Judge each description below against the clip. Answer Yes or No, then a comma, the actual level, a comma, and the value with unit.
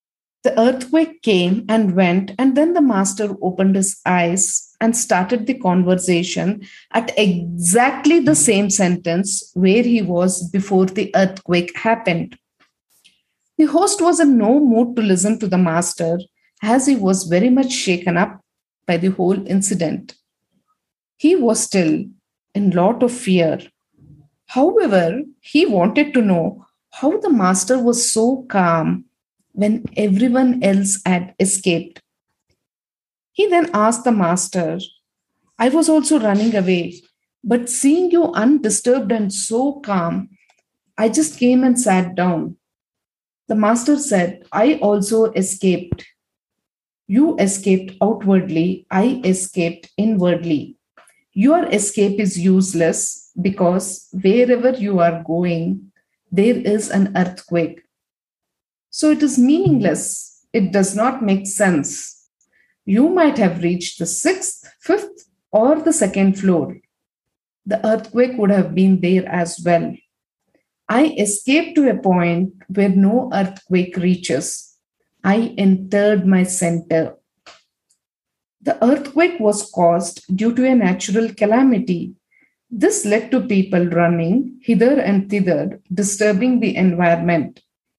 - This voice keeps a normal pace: No, slow, 125 wpm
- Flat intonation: No, average, 5.1 semitones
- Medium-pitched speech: No, high, 200 Hz